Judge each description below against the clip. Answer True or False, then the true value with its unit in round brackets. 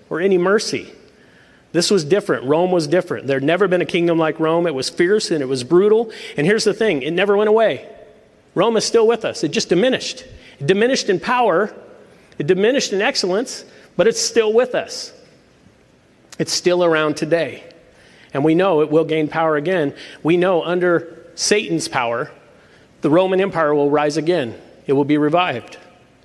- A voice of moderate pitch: True (175 Hz)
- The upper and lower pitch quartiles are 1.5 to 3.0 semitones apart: False (4.7 semitones)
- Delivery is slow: False (185 wpm)